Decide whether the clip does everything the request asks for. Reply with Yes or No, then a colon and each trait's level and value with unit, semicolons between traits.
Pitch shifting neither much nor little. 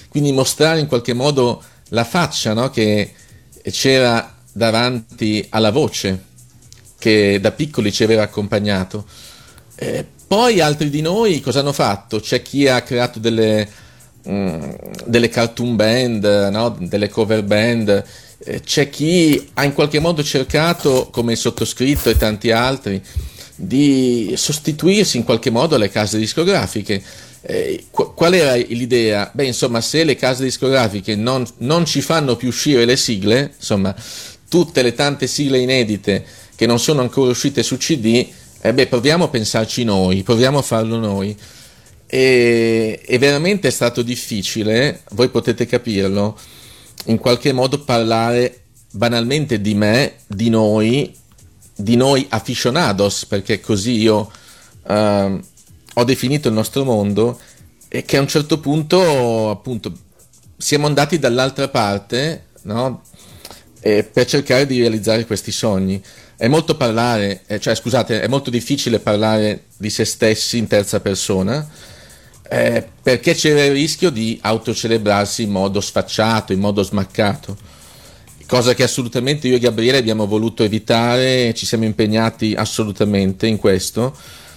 Yes: average, 3.6 semitones